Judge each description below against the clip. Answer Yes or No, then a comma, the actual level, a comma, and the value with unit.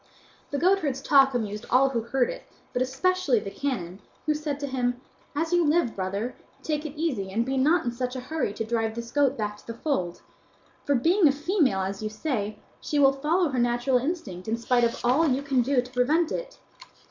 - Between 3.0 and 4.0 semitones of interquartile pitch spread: No, average, 4.4 semitones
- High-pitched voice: Yes, very high, 260 Hz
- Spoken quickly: Yes, fast, 215 wpm